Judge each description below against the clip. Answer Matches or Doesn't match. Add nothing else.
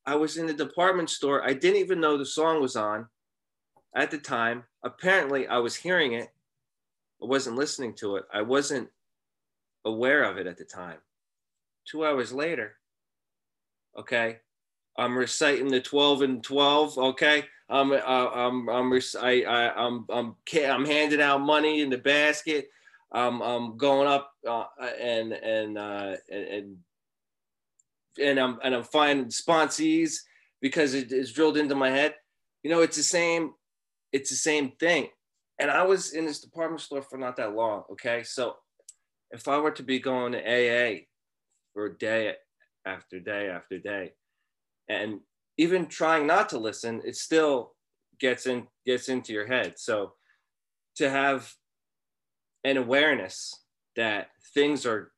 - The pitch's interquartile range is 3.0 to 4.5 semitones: Matches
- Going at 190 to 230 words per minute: Doesn't match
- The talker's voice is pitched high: Doesn't match